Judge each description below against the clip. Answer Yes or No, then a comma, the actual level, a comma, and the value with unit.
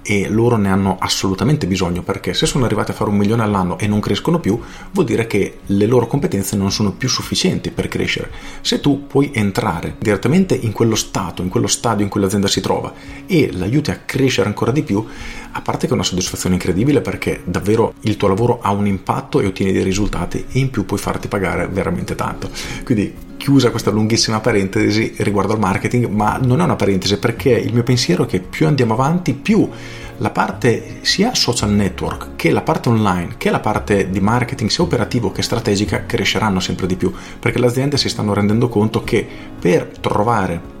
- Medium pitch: No, low, 105 Hz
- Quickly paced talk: Yes, fast, 200 wpm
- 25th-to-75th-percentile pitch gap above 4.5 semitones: No, average, 3.8 semitones